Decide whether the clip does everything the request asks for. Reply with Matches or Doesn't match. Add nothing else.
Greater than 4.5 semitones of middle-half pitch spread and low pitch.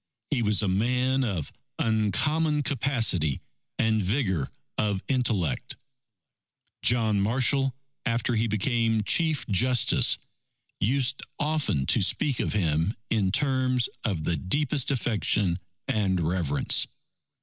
Matches